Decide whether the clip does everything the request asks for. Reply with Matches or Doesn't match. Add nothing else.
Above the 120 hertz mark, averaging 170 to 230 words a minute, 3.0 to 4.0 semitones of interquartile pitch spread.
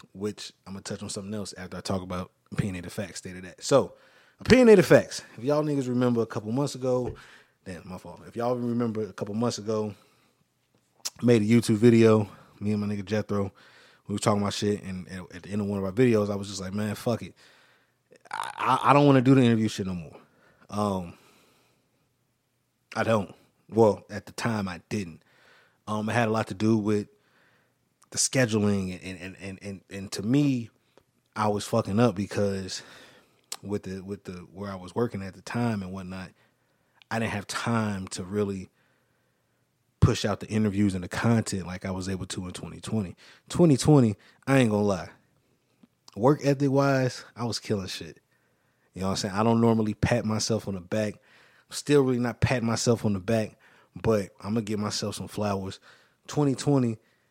Doesn't match